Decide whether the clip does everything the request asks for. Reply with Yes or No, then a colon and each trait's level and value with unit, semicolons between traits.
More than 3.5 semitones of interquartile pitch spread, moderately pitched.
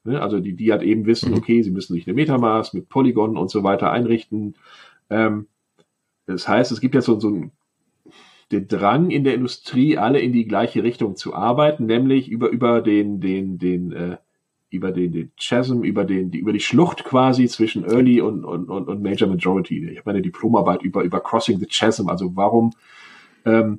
No: average, 3.9 semitones; low, 110 Hz